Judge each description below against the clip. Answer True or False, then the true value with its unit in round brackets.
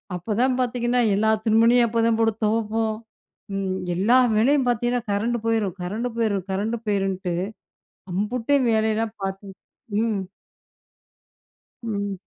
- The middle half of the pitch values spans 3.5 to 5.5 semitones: False (2.7 semitones)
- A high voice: True (220 Hz)